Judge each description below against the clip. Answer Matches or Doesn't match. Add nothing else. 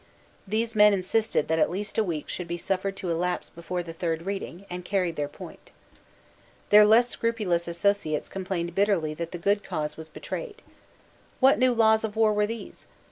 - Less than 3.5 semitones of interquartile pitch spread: Doesn't match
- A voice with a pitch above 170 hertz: Matches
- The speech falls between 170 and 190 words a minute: Matches